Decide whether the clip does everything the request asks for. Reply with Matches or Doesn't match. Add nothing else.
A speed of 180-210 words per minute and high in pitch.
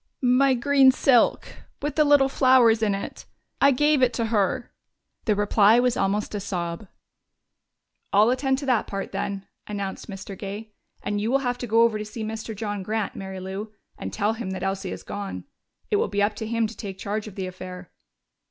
Matches